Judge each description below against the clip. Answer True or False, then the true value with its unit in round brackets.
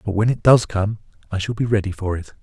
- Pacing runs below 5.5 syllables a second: False (6.2 syllables/s)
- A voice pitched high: False (100 Hz)